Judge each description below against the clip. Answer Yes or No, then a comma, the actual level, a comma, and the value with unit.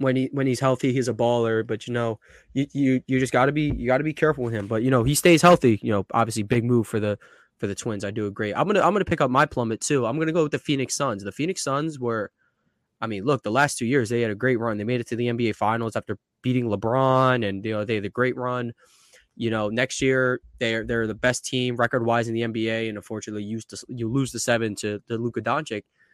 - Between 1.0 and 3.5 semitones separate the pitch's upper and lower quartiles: Yes, average, 2.8 semitones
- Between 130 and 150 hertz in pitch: No, low, 120 Hz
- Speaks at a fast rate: Yes, fast, 275 wpm